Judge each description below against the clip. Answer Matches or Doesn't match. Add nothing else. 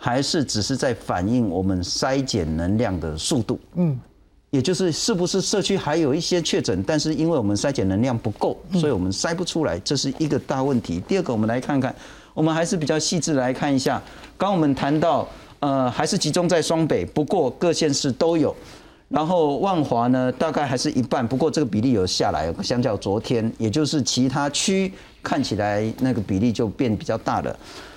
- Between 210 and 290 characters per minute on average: Doesn't match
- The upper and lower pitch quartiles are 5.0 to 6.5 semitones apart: Matches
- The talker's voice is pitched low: Doesn't match